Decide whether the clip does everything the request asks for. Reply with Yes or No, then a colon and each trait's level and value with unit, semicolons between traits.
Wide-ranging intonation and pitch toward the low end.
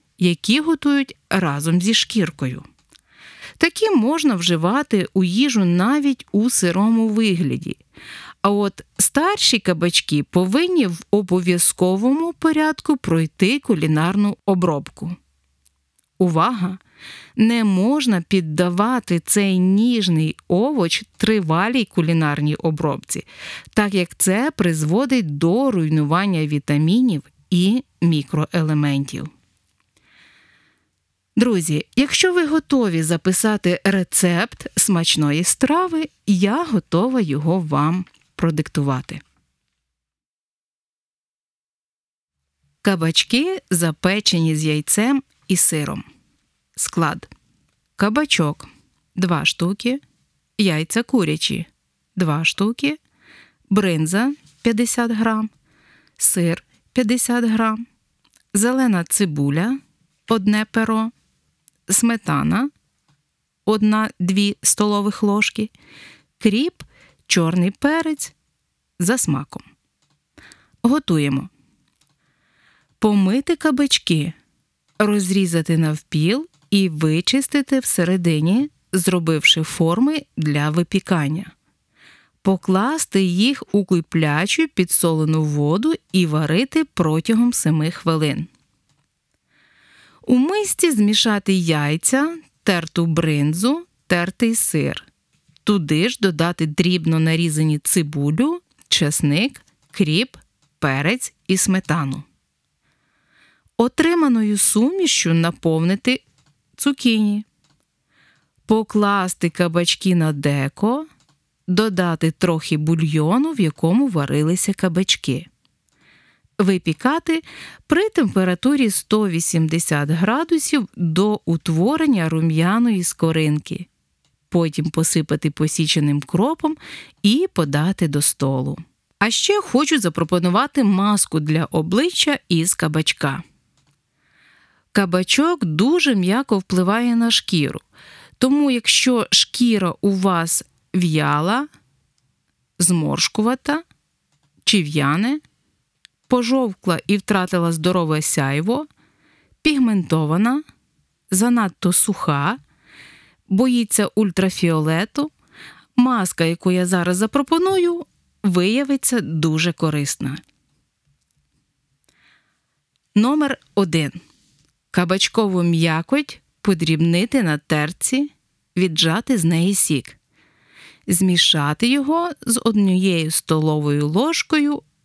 No: wide, 6.4 semitones; medium, 185 Hz